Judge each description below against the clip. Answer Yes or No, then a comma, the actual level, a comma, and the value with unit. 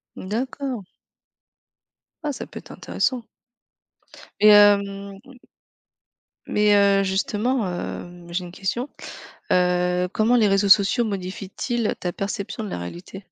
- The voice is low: No, high, 200 Hz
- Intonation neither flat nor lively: Yes, average, 3.0 semitones